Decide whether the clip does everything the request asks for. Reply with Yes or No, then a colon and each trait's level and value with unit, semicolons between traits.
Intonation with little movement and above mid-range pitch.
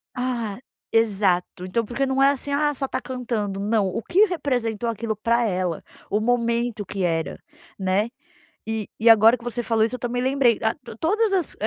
No: average, 3.4 semitones; high, 230 Hz